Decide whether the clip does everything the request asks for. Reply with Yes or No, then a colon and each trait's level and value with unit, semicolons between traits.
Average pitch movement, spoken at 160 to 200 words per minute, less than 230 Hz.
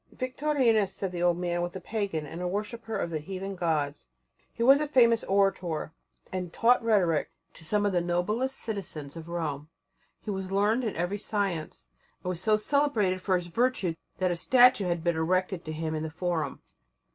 Yes: average, 4.2 semitones; average, 190 wpm; medium, 185 Hz